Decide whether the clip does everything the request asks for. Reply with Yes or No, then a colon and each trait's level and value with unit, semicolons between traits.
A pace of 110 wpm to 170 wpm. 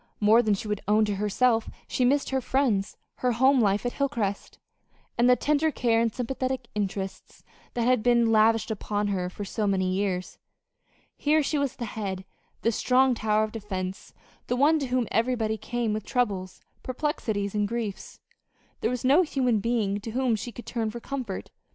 No: average, 180 wpm